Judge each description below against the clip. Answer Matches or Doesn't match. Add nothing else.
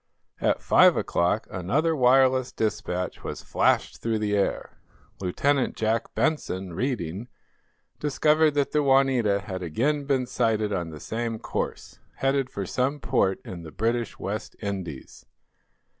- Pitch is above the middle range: Doesn't match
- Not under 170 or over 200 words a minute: Doesn't match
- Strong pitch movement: Matches